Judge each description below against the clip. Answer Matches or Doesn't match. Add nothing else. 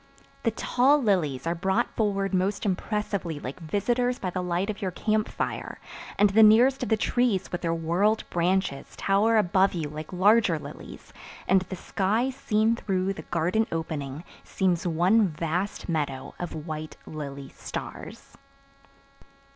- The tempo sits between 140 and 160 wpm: Matches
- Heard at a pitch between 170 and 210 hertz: Matches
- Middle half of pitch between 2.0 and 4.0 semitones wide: Doesn't match